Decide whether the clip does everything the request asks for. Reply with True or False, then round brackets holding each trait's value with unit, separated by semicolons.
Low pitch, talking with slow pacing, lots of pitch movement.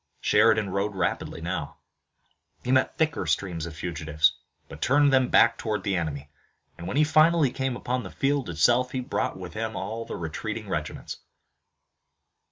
False (110 Hz; 165 wpm; 7.1 semitones)